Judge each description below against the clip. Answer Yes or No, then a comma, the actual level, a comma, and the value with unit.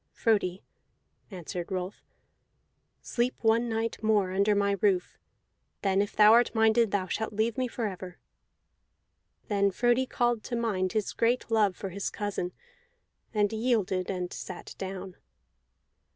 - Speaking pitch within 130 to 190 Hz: No, high, 205 Hz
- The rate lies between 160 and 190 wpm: No, slow, 135 wpm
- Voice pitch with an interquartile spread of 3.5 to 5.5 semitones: No, average, 3.1 semitones